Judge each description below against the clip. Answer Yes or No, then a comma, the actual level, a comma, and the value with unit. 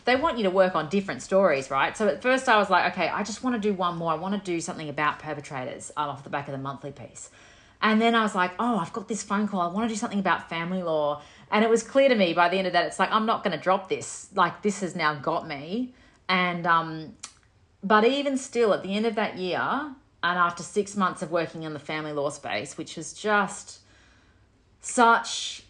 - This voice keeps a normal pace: No, fast, 250 wpm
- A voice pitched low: No, medium, 185 Hz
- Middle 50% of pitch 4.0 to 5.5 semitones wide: Yes, average, 5.2 semitones